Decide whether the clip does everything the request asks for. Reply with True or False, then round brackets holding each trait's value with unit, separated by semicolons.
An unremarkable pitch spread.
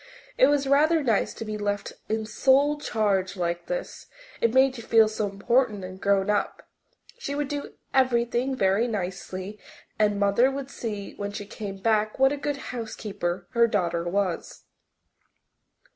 True (4.8 semitones)